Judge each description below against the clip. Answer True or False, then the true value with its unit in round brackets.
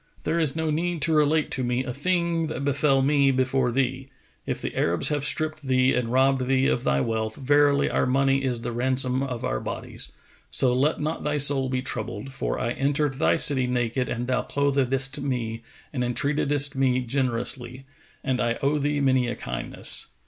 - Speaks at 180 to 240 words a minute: True (190 wpm)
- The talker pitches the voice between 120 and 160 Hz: True (135 Hz)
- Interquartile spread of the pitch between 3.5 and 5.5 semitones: False (2.4 semitones)